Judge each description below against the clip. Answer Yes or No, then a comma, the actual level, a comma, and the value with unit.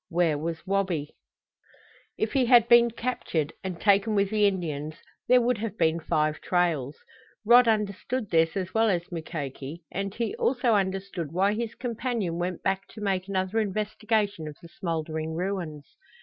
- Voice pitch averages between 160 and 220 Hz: Yes, high, 190 Hz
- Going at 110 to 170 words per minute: Yes, average, 160 wpm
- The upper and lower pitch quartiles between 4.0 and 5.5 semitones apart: Yes, average, 4.7 semitones